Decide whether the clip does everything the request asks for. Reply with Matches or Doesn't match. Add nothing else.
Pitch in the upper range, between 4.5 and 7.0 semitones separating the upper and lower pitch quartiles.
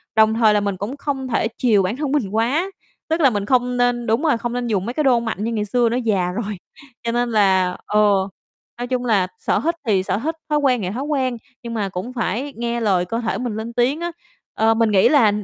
Doesn't match